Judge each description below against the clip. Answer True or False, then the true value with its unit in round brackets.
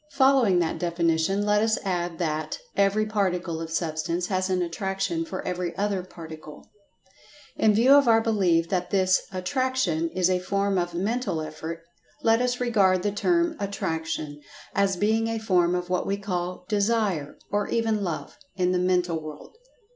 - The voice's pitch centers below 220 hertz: True (185 Hz)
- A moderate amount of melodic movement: True (3.6 semitones)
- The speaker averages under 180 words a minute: True (160 wpm)